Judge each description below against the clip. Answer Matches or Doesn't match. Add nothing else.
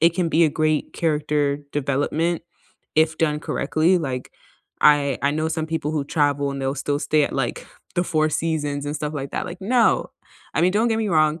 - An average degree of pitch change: Doesn't match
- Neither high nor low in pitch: Matches